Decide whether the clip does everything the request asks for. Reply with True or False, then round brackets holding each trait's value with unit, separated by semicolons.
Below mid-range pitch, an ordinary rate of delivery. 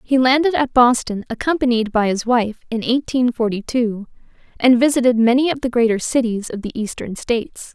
False (240 Hz; 180 wpm)